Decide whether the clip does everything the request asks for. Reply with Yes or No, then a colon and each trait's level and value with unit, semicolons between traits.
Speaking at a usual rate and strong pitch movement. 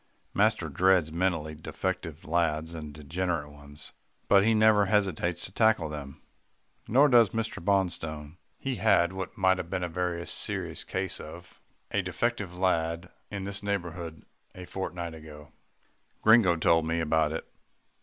No: average, 145 wpm; average, 3.5 semitones